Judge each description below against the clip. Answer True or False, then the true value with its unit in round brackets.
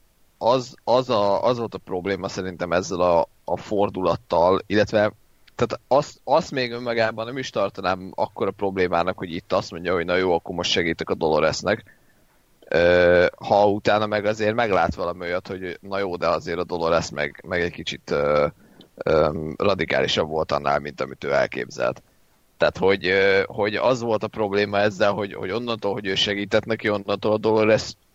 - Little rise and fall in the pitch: False (3.0 semitones)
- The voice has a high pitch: False (100 Hz)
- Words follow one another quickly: True (175 wpm)